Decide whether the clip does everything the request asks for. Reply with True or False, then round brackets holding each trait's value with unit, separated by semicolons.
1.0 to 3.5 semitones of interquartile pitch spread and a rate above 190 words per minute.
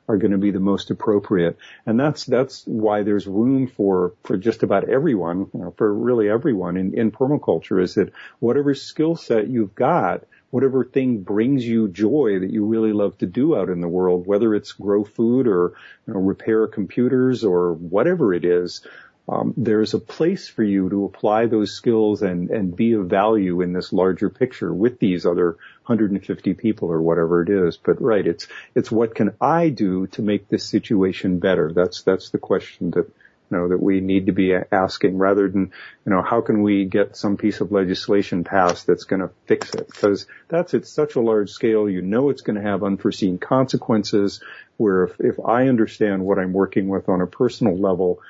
True (2.9 semitones; 200 wpm)